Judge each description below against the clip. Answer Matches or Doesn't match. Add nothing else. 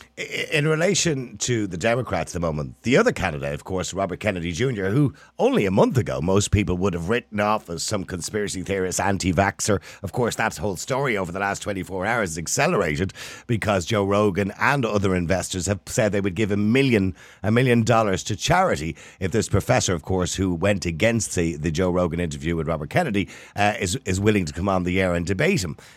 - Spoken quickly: Matches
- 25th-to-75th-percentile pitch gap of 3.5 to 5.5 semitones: Doesn't match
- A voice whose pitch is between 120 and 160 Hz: Doesn't match